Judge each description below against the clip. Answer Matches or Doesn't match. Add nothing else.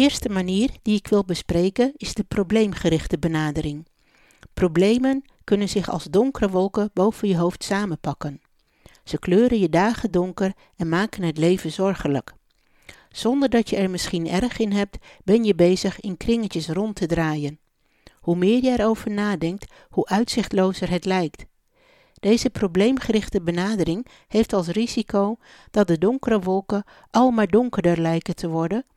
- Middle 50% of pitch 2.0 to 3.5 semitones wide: Doesn't match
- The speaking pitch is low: Doesn't match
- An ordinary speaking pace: Matches